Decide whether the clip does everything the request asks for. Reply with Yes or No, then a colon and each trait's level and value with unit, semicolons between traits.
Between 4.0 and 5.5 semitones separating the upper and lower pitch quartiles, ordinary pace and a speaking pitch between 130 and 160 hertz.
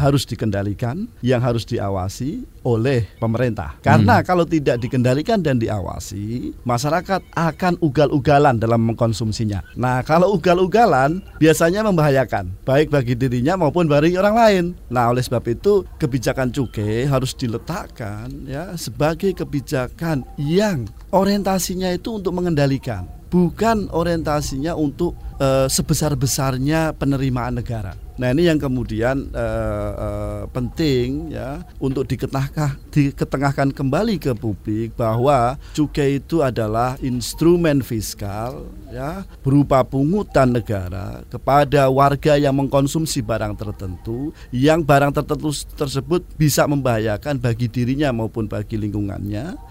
Yes: average, 4.9 semitones; average, 115 wpm; low, 135 Hz